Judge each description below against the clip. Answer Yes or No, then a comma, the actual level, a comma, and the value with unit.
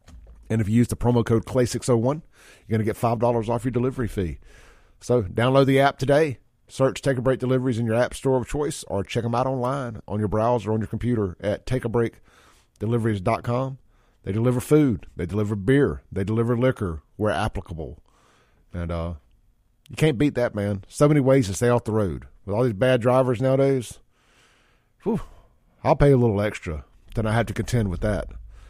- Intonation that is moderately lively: Yes, average, 3.9 semitones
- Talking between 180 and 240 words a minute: Yes, average, 190 wpm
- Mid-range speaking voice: No, low, 115 Hz